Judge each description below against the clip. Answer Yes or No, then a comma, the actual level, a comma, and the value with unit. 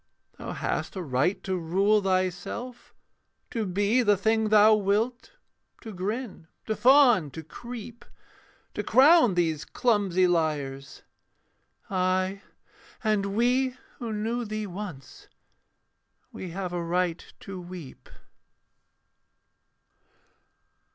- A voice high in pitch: Yes, high, 200 Hz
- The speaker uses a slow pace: Yes, slow, 105 wpm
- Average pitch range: Yes, average, 4.0 semitones